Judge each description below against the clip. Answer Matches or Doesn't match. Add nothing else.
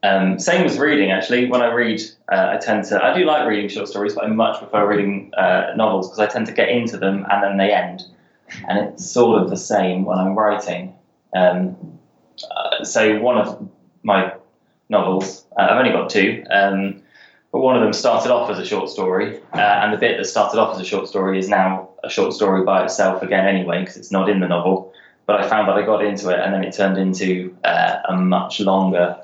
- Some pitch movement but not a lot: Doesn't match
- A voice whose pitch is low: Matches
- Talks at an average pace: Doesn't match